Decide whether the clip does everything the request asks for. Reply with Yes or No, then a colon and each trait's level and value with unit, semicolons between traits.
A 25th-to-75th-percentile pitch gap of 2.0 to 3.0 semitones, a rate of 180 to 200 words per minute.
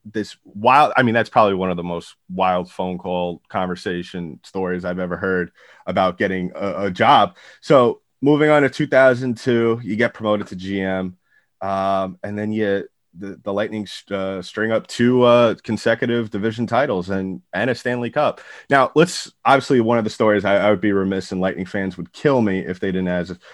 No: average, 4.1 semitones; average, 190 wpm